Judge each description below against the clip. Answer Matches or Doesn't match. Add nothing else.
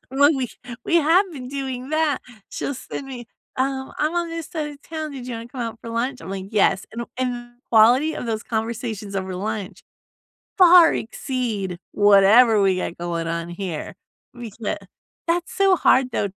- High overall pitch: Matches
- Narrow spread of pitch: Doesn't match